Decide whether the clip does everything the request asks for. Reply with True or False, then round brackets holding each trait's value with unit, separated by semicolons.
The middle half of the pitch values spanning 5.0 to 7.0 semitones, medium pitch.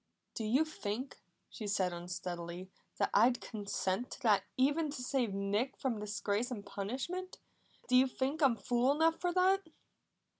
False (5.5 semitones; 245 Hz)